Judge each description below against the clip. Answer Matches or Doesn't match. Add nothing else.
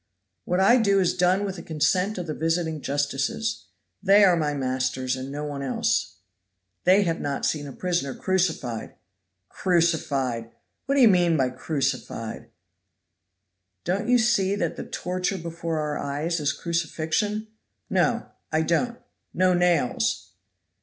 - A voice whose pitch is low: Doesn't match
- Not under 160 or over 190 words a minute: Doesn't match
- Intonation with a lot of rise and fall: Doesn't match